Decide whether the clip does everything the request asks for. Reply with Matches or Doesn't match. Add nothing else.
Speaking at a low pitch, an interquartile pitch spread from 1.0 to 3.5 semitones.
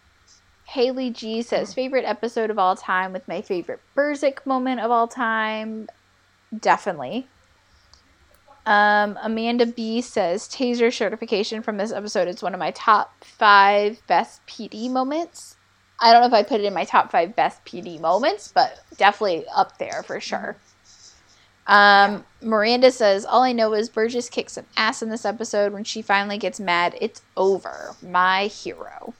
Doesn't match